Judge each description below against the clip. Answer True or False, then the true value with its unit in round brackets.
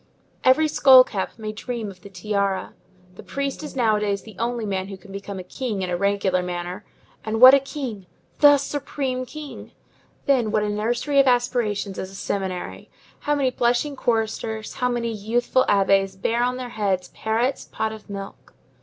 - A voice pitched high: True (220 Hz)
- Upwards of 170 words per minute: True (180 wpm)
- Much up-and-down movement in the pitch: False (4.2 semitones)